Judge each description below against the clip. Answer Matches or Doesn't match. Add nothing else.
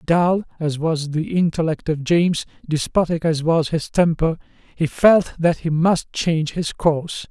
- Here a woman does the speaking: Doesn't match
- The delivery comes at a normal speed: Matches